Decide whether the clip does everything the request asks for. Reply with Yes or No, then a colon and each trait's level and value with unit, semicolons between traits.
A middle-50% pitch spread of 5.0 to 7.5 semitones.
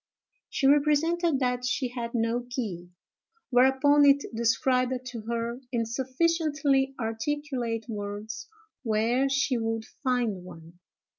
No: average, 3.3 semitones